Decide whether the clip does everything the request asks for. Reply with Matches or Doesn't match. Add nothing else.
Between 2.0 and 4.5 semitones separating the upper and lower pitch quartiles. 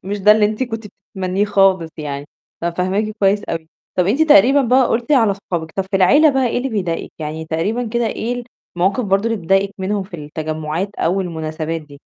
Doesn't match